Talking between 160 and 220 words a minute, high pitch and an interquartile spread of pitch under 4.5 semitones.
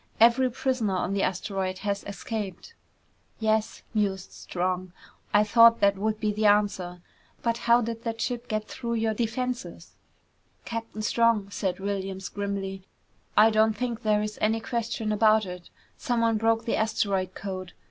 No: average, 150 wpm; high, 215 Hz; average, 2.7 semitones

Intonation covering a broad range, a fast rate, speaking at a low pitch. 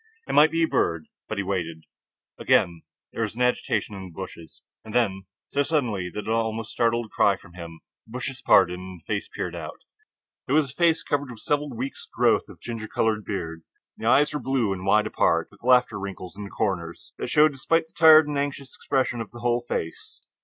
Yes: wide, 6.0 semitones; fast, 215 wpm; low, 115 Hz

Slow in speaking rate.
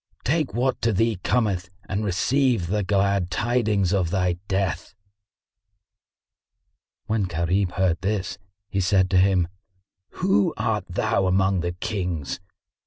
Yes: slow, 125 wpm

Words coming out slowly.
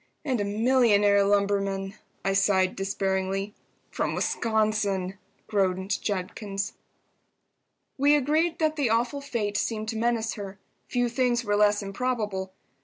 Yes: slow, 120 wpm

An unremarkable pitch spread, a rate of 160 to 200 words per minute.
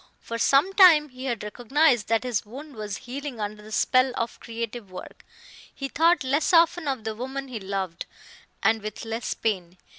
Yes: average, 4.5 semitones; average, 180 wpm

